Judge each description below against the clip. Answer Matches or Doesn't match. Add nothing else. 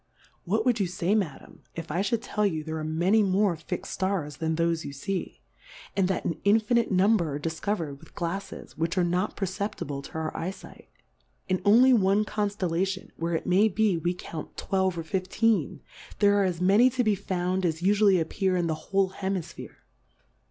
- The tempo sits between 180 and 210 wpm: Matches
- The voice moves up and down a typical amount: Matches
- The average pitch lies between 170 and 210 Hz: Matches